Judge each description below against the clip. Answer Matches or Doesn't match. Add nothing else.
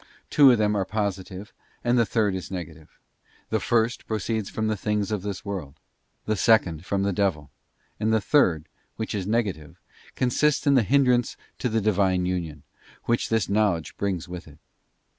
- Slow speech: Doesn't match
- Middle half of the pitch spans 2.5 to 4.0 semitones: Matches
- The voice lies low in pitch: Matches